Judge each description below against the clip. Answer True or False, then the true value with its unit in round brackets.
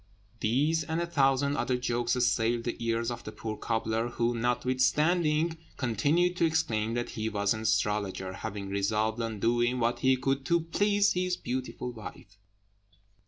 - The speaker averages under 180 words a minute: True (160 wpm)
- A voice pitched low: True (120 Hz)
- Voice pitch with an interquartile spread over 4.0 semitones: True (4.8 semitones)